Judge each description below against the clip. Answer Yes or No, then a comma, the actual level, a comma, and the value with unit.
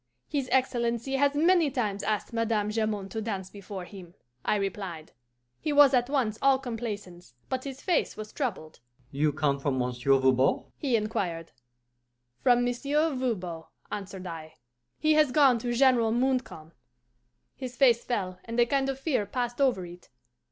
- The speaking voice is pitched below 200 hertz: No, high, 230 Hz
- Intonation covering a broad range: Yes, wide, 6.1 semitones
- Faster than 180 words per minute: No, average, 160 wpm